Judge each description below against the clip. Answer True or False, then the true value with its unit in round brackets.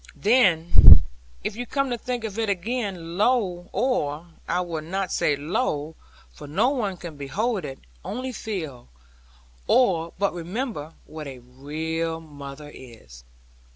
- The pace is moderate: False (130 wpm)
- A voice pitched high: False (175 Hz)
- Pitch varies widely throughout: True (6.6 semitones)